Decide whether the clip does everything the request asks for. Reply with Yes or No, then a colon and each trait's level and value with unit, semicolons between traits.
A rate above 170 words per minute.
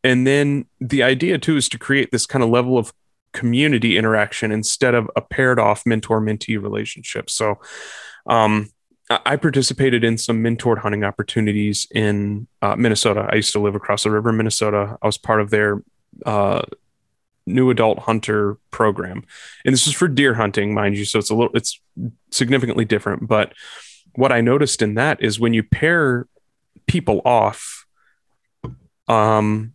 No: average, 165 wpm